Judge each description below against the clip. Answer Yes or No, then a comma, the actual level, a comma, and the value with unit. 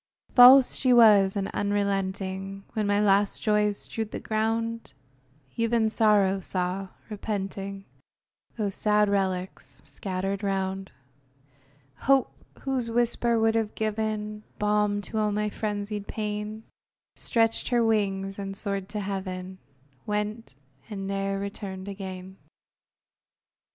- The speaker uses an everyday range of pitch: No, narrow, 1.9 semitones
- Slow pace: Yes, slow, 115 wpm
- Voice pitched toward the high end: Yes, high, 205 Hz